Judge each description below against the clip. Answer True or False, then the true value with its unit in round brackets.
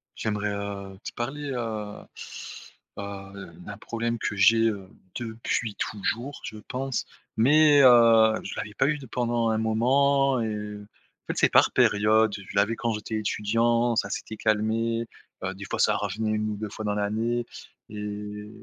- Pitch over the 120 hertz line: False (110 Hz)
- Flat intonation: True (2.2 semitones)